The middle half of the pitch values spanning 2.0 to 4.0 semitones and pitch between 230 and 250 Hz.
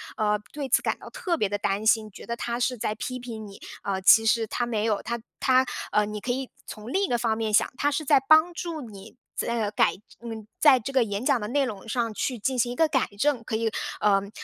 Yes: average, 3.7 semitones; high, 235 Hz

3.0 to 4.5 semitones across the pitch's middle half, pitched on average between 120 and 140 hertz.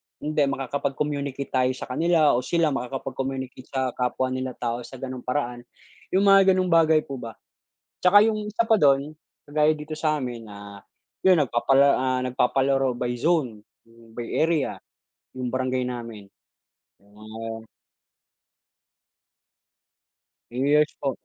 Yes: average, 3.6 semitones; low, 135 Hz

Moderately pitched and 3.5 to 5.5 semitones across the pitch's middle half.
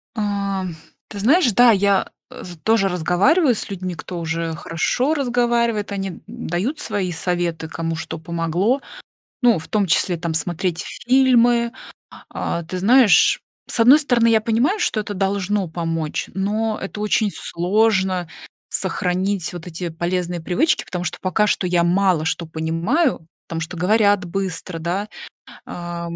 No: high, 195 Hz; average, 4.5 semitones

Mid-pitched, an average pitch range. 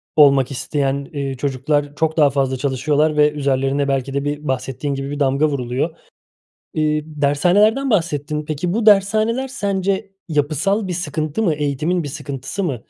Yes: medium, 150 Hz; average, 3.9 semitones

